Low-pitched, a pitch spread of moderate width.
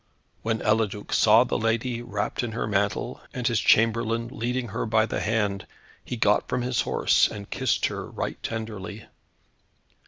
No: low, 110 Hz; narrow, 1.9 semitones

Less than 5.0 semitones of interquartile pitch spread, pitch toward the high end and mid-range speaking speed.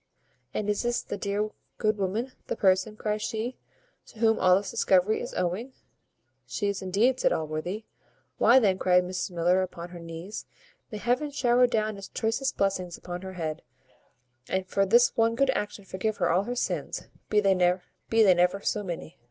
Yes: average, 3.5 semitones; high, 200 Hz; average, 175 wpm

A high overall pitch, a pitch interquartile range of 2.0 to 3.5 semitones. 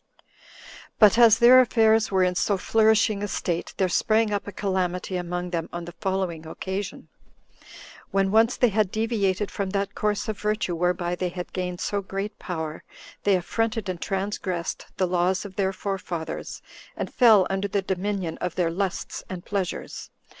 Yes: high, 195 Hz; narrow, 2.6 semitones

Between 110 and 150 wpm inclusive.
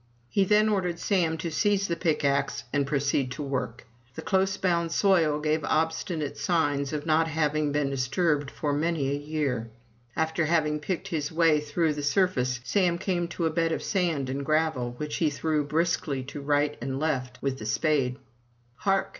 No: average, 180 wpm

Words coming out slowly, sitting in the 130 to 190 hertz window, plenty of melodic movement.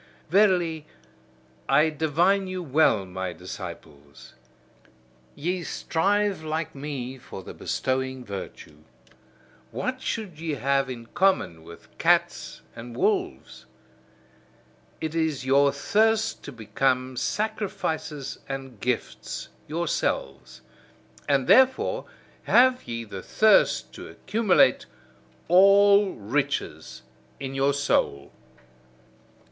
Yes: slow, 100 wpm; medium, 140 Hz; wide, 7.5 semitones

